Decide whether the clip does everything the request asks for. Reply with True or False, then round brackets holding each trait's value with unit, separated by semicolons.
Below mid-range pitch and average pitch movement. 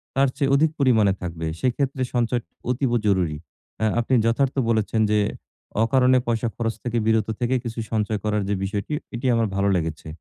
True (115 Hz; 3.3 semitones)